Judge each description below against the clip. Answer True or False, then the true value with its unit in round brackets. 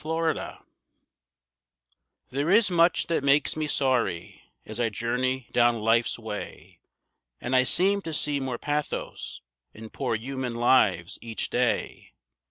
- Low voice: True (130 Hz)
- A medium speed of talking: False (130 wpm)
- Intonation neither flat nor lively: True (4.4 semitones)